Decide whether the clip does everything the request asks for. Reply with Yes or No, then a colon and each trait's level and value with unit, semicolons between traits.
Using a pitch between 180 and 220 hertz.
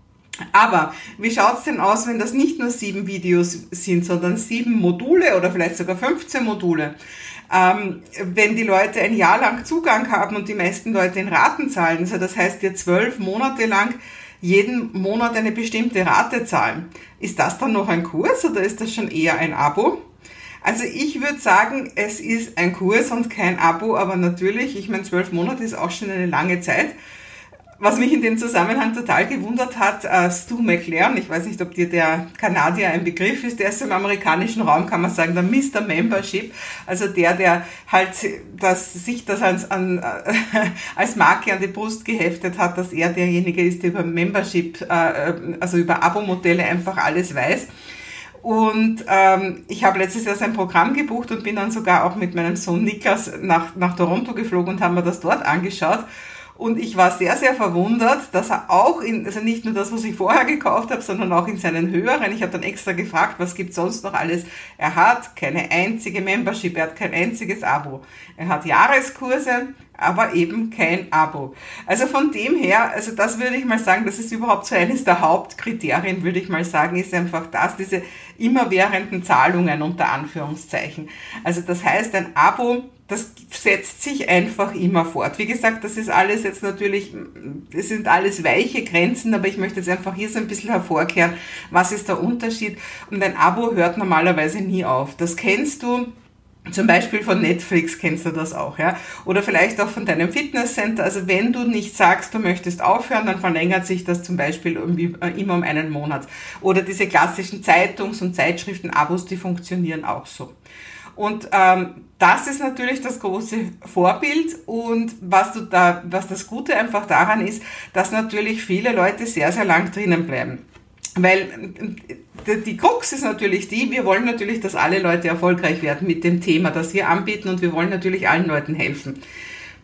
Yes: high, 190 Hz